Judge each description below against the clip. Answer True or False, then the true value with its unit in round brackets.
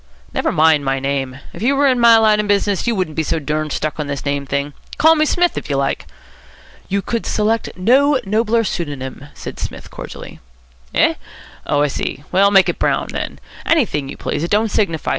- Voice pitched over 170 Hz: True (185 Hz)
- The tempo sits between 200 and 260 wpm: True (205 wpm)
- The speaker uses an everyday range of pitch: False (7.9 semitones)